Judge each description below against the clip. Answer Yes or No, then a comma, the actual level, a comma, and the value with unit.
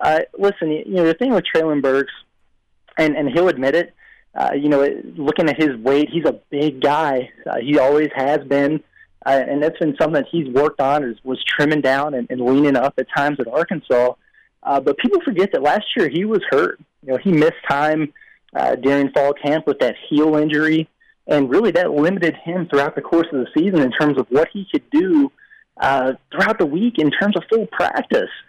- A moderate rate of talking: No, fast, 210 wpm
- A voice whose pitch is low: No, medium, 150 Hz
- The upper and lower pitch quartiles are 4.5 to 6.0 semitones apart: No, average, 3.4 semitones